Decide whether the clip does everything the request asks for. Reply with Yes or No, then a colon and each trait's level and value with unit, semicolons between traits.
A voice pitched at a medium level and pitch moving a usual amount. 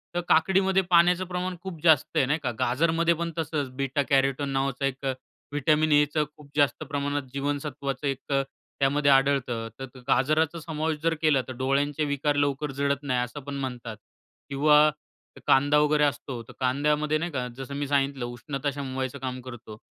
No: medium, 145 Hz; narrow, 2.2 semitones